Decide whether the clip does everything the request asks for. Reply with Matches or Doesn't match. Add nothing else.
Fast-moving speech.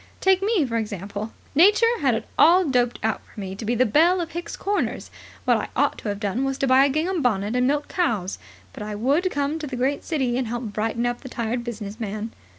Matches